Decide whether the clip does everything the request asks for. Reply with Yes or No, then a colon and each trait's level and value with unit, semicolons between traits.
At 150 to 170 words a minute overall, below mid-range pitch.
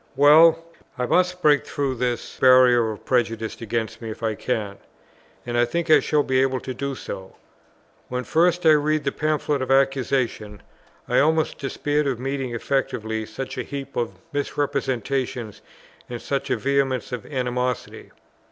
Yes: average, 160 wpm; low, 130 Hz